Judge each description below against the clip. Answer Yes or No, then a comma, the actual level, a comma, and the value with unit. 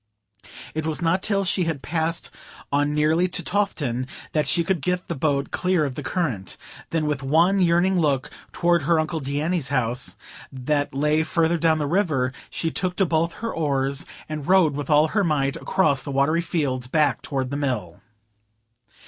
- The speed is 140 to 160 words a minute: No, average, 180 wpm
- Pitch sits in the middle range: Yes, medium, 155 Hz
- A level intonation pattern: No, average, 3.6 semitones